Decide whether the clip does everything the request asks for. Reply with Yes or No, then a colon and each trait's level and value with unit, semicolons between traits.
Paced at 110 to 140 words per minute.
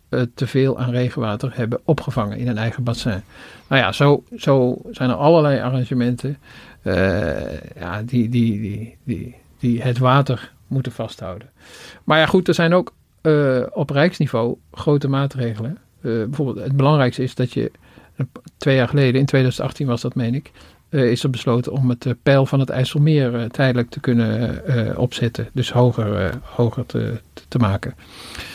No: average, 165 wpm